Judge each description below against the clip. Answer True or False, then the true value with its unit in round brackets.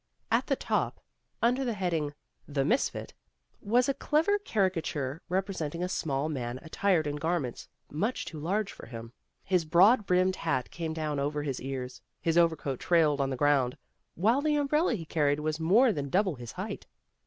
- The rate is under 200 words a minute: True (175 wpm)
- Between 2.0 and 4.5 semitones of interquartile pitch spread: False (5.4 semitones)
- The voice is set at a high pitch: False (165 Hz)